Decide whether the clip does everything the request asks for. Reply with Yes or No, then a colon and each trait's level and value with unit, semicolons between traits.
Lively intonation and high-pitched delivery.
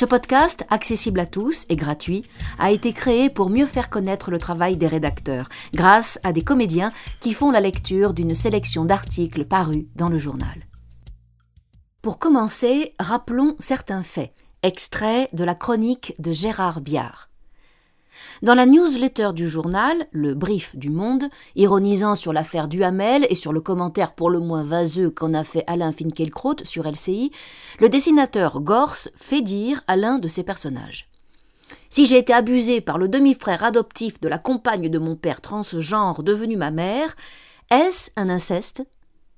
Yes: wide, 6.8 semitones; high, 195 Hz